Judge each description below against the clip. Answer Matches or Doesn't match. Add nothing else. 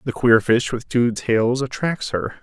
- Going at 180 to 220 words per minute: Matches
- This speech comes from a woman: Doesn't match